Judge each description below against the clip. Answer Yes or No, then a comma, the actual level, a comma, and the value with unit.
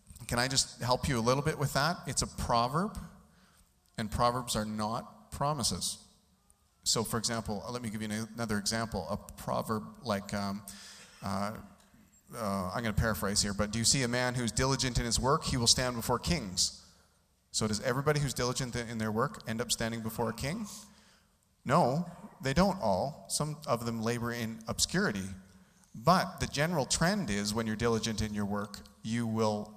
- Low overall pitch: Yes, low, 115 Hz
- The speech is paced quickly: No, average, 185 wpm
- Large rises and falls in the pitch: No, average, 3.1 semitones